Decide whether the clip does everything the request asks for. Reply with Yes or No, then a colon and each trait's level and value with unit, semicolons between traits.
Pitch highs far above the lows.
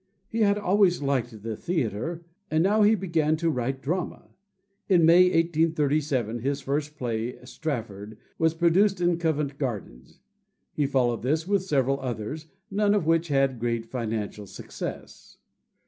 Yes: wide, 5.8 semitones